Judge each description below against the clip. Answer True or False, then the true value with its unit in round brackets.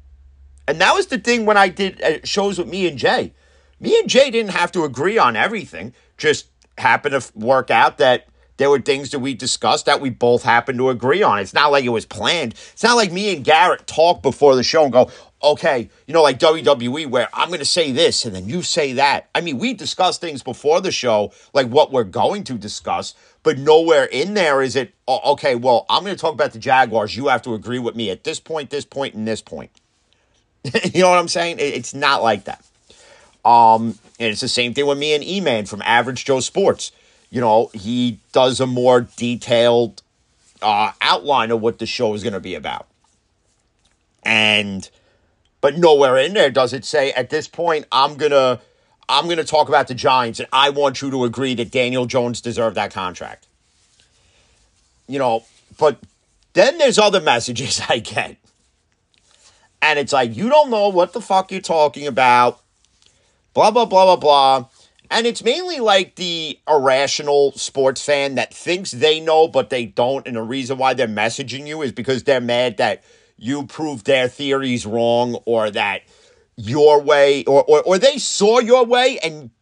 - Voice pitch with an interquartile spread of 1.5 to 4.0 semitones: False (5.3 semitones)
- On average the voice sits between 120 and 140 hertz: True (135 Hz)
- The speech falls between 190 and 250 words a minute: True (195 wpm)